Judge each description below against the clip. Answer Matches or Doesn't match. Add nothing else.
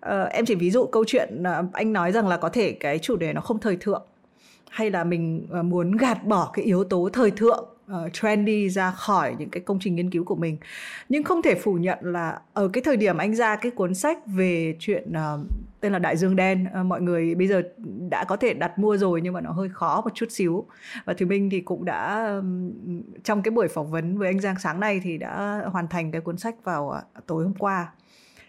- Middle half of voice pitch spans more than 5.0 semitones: Doesn't match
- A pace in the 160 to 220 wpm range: Doesn't match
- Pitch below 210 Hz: Matches